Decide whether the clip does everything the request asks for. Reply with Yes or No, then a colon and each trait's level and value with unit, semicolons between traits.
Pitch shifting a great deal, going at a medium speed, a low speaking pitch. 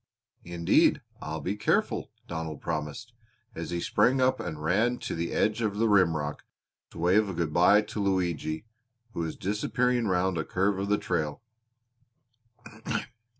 No: average, 4.4 semitones; average, 150 wpm; very low, 95 Hz